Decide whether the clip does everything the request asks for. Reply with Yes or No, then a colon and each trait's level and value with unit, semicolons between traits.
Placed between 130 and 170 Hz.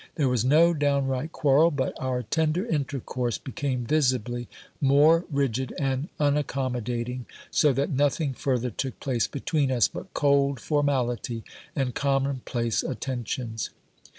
Yes: low, 135 Hz